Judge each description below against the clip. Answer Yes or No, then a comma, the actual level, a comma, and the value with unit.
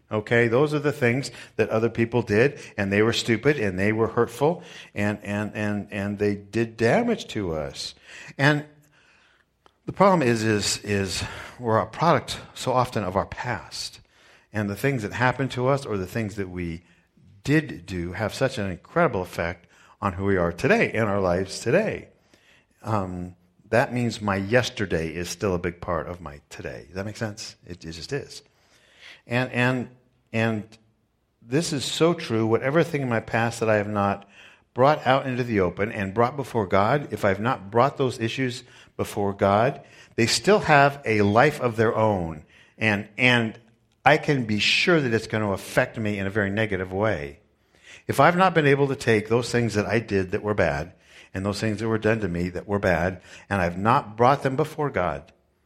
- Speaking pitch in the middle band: No, low, 110 Hz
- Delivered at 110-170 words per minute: No, average, 195 wpm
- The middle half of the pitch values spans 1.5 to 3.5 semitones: No, average, 4.0 semitones